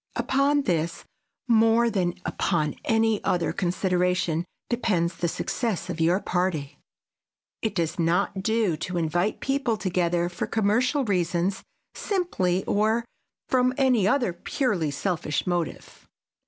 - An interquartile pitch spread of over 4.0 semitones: Yes, average, 4.7 semitones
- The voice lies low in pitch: No, medium, 185 Hz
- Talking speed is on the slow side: Yes, slow, 120 wpm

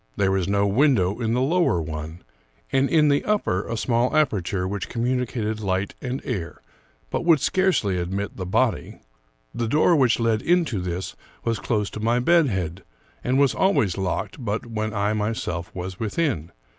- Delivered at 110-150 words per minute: No, average, 170 wpm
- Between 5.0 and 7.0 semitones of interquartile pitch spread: Yes, wide, 5.6 semitones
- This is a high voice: No, low, 110 Hz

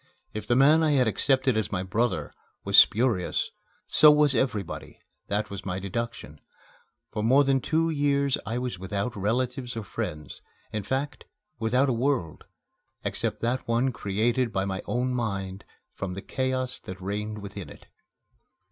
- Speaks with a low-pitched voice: Yes, low, 115 Hz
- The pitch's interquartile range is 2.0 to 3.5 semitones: No, average, 4.7 semitones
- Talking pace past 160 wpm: No, average, 155 wpm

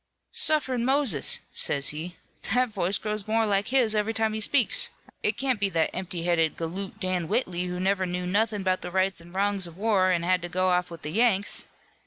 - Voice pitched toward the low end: No, high, 190 Hz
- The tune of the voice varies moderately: Yes, average, 3.6 semitones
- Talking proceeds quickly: Yes, fast, 215 wpm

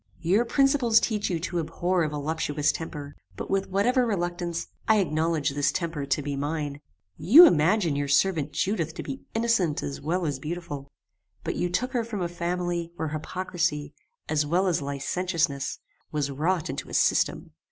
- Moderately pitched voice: Yes, medium, 170 Hz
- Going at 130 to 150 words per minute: No, average, 170 wpm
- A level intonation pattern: No, average, 4.1 semitones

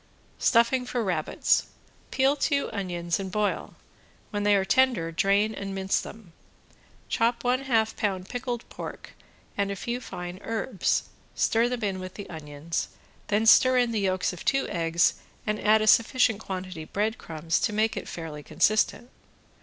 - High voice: Yes, high, 205 Hz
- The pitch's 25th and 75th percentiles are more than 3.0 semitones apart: Yes, average, 4.1 semitones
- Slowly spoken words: No, average, 155 wpm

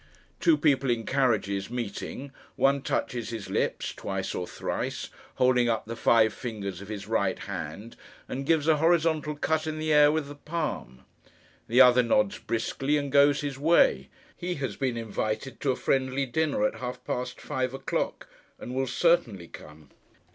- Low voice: Yes, low, 130 Hz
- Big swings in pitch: No, average, 4.8 semitones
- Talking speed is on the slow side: No, average, 170 wpm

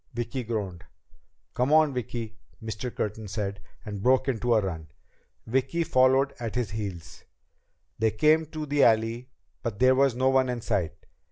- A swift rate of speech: No, average, 160 wpm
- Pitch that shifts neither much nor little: Yes, average, 3.6 semitones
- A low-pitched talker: Yes, low, 120 Hz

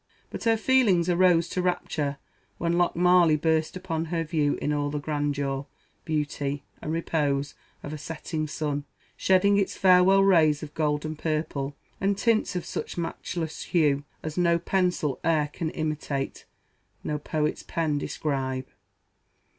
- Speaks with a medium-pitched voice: Yes, medium, 155 Hz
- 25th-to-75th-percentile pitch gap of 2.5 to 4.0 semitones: Yes, average, 3.2 semitones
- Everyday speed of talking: Yes, average, 145 wpm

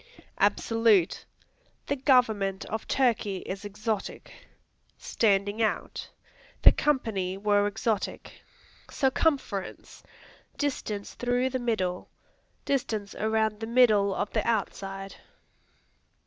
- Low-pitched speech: No, high, 215 Hz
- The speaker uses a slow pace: Yes, slow, 90 wpm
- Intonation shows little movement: No, average, 3.5 semitones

